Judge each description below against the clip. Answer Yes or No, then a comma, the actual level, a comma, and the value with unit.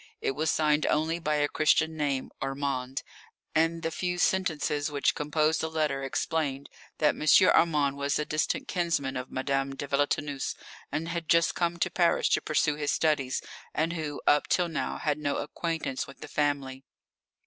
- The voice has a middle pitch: Yes, medium, 150 Hz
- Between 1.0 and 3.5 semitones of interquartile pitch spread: Yes, narrow, 2.5 semitones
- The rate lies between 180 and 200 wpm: No, average, 170 wpm